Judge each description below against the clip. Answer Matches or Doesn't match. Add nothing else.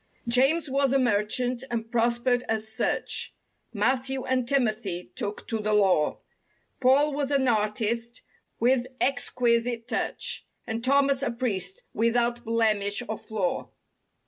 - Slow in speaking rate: Matches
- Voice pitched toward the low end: Doesn't match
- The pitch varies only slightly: Doesn't match